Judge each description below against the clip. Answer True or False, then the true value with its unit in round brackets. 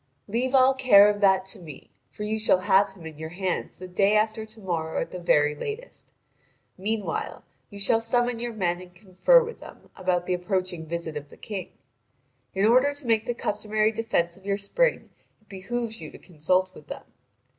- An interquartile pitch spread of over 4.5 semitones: False (3.9 semitones)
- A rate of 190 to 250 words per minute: True (200 wpm)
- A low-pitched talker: False (200 Hz)